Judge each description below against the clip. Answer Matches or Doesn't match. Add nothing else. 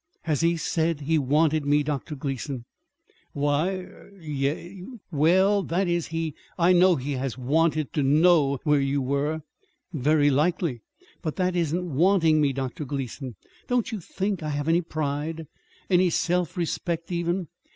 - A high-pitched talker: Doesn't match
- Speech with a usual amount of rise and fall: Matches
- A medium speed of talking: Matches